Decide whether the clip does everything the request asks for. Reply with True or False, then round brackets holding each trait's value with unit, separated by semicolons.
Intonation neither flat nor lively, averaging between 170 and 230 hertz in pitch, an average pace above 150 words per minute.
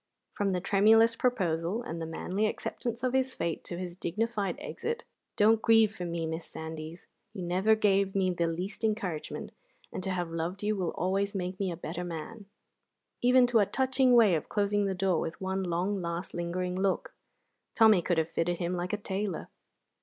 True (3.9 semitones; 190 Hz; 190 wpm)